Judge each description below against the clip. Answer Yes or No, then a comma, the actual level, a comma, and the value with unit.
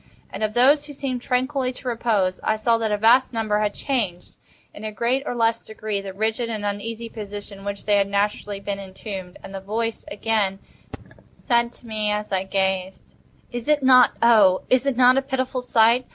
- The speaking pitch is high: Yes, high, 220 Hz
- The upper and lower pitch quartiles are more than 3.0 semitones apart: Yes, average, 3.5 semitones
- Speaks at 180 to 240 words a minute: Yes, average, 195 wpm